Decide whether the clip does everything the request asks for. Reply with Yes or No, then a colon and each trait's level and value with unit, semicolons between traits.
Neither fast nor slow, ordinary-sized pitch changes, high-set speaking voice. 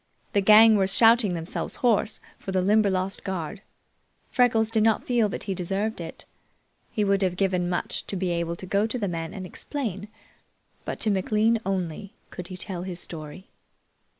Yes: average, 180 wpm; average, 3.1 semitones; high, 195 Hz